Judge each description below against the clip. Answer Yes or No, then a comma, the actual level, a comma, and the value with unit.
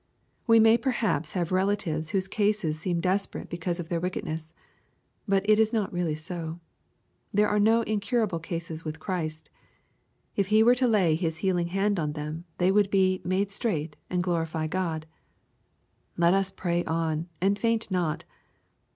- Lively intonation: No, average, 3.8 semitones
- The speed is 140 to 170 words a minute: Yes, average, 160 wpm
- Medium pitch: Yes, medium, 180 Hz